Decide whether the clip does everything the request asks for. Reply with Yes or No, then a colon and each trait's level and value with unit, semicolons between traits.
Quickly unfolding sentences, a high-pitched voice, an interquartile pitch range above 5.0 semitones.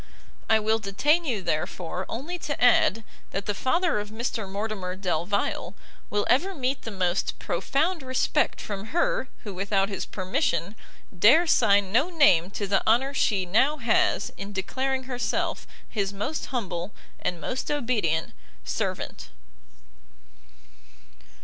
No: slow, 135 wpm; high, 215 Hz; wide, 5.5 semitones